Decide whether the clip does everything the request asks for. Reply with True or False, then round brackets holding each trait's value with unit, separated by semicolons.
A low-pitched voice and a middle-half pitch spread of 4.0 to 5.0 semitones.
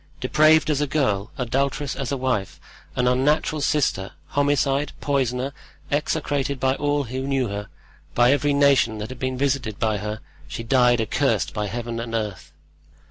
False (130 Hz; 3.6 semitones)